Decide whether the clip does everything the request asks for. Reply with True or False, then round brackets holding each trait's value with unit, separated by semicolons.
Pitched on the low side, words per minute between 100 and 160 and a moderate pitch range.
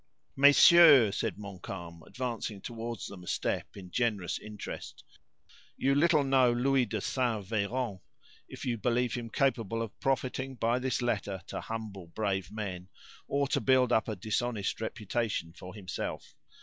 True (115 Hz; 150 wpm; 4.1 semitones)